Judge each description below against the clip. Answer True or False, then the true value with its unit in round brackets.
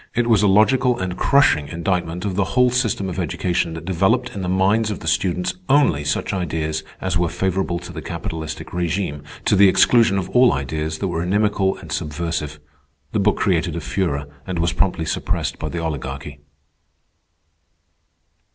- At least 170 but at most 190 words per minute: True (175 wpm)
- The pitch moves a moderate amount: True (3.6 semitones)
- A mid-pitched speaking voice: False (90 Hz)